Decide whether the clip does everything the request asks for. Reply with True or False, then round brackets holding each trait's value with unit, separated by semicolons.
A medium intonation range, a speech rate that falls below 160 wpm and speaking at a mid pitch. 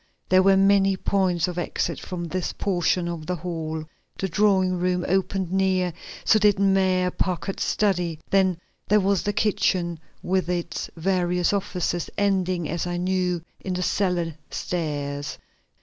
False (1.9 semitones; 150 wpm; 180 Hz)